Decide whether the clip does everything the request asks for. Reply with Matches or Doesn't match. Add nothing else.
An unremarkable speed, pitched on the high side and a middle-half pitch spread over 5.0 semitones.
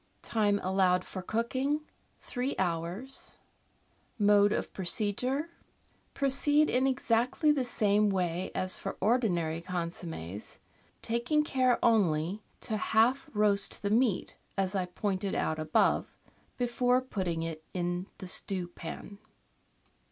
Doesn't match